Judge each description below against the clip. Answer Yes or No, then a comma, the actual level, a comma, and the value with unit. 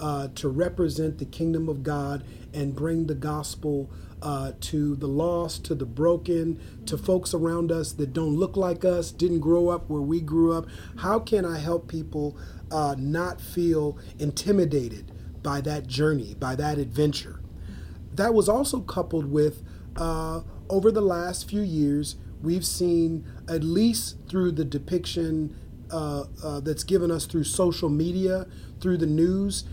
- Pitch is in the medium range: Yes, medium, 160 Hz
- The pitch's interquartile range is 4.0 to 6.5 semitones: No, average, 3.1 semitones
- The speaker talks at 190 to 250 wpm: No, average, 155 wpm